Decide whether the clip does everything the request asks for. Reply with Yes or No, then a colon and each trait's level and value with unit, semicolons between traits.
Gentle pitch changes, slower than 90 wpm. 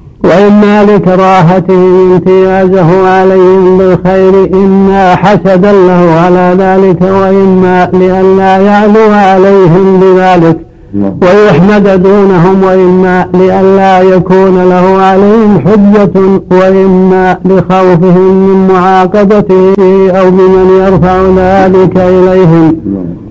Yes: narrow, 0.7 semitones; average, 80 wpm